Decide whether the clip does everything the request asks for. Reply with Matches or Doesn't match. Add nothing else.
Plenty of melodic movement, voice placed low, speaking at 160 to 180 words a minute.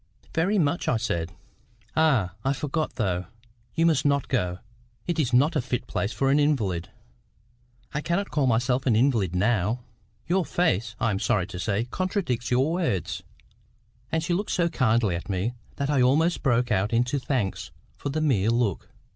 Matches